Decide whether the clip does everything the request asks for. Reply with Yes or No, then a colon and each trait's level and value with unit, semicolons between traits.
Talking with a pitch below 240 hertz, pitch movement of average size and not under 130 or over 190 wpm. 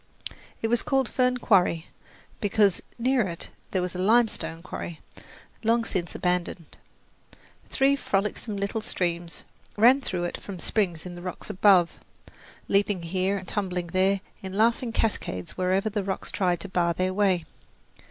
Yes: high, 190 Hz; average, 3.5 semitones; average, 150 wpm